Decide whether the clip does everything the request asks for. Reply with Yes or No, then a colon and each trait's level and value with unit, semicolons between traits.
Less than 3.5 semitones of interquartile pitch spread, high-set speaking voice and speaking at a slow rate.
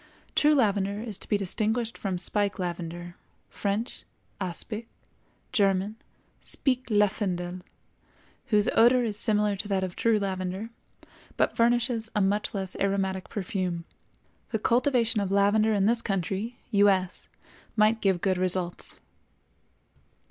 Yes: average, 2.8 semitones; high, 205 Hz; slow, 125 wpm